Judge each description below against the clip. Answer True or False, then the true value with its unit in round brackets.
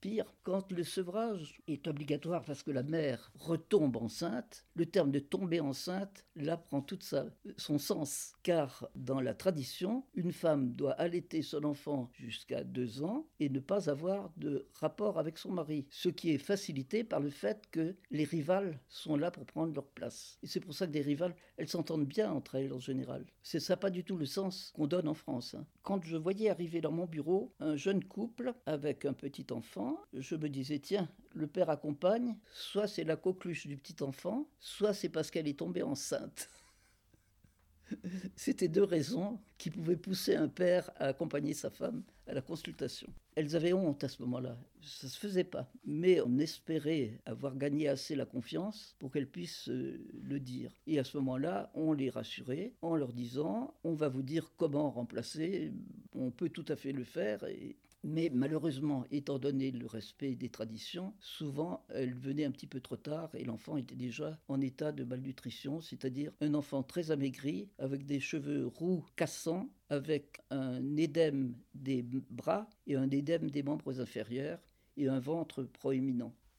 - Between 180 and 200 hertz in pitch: False (150 Hz)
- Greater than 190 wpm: False (180 wpm)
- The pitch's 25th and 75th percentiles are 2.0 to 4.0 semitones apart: False (4.8 semitones)